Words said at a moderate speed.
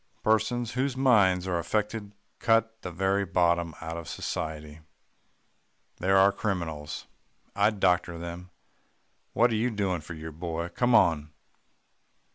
No: slow, 130 wpm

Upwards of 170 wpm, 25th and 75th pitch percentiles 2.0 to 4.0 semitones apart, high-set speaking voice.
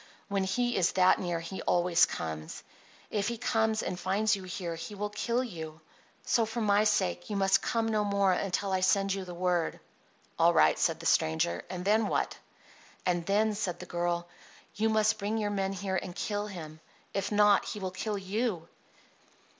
Yes: average, 190 wpm; average, 3.0 semitones; high, 195 Hz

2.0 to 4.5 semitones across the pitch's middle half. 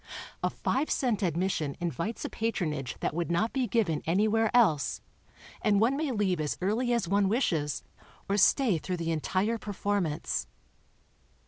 No: average, 5.2 semitones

